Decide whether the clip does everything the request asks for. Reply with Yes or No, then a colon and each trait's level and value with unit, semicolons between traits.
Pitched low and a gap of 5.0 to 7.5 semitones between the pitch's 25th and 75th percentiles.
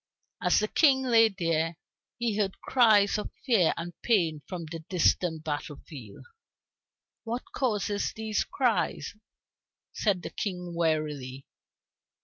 No: medium, 185 Hz; wide, 5.4 semitones